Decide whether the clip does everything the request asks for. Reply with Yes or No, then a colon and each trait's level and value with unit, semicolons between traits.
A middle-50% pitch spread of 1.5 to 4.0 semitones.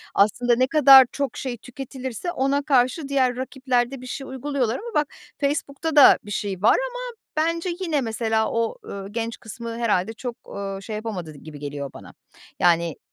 No: average, 4.5 semitones